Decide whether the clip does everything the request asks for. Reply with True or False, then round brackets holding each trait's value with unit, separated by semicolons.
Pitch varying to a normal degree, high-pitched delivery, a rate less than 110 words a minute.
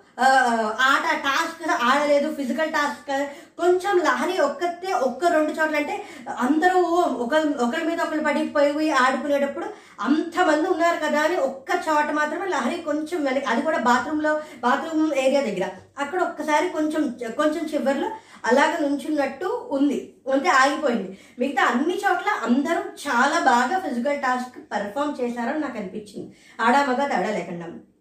False (3.5 semitones; 295 Hz; 120 wpm)